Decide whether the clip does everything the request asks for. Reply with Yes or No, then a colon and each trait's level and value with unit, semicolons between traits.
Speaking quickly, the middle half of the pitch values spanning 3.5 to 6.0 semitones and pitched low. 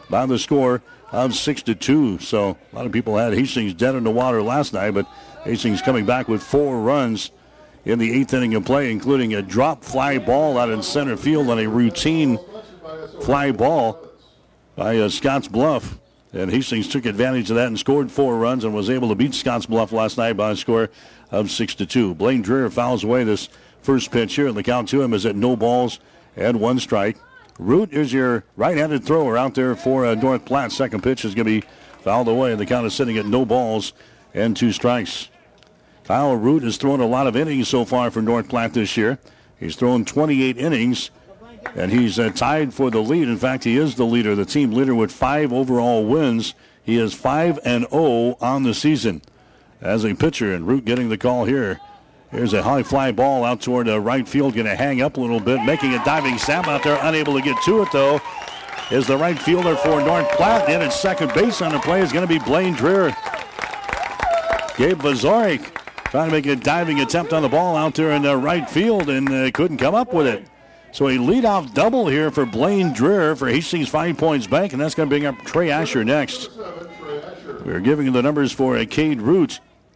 Yes: fast, 210 wpm; average, 3.8 semitones; low, 130 Hz